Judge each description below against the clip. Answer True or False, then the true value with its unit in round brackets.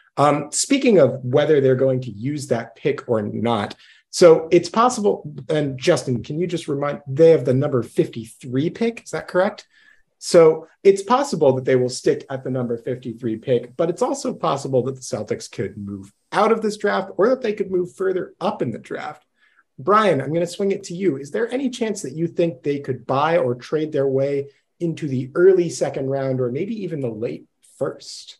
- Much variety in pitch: True (6.1 semitones)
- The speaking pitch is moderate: True (150 Hz)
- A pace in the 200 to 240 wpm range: True (205 wpm)